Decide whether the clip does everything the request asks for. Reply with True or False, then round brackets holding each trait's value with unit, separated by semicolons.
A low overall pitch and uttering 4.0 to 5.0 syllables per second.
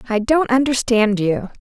False (235 Hz; 4.5 syllables/s)